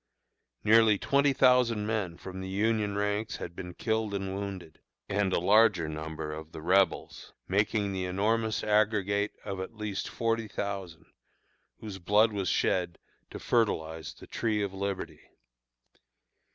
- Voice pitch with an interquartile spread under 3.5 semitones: Yes, average, 2.7 semitones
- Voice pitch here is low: Yes, low, 100 Hz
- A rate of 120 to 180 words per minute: Yes, average, 140 wpm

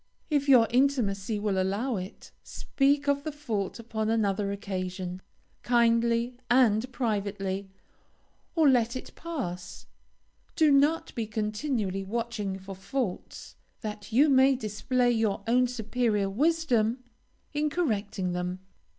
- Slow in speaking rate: Yes, slow, 120 wpm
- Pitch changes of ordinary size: Yes, average, 4.7 semitones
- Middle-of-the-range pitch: No, high, 225 Hz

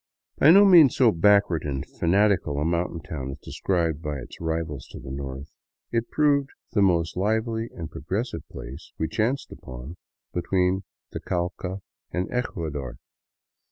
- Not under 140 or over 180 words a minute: Yes, average, 155 wpm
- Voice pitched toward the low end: Yes, very low, 85 Hz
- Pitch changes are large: Yes, wide, 6.1 semitones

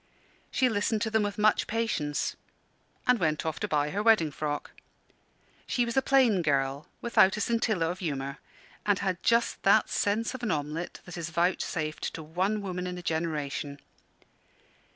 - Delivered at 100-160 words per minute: No, average, 170 wpm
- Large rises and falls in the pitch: Yes, wide, 6.0 semitones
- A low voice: No, medium, 180 Hz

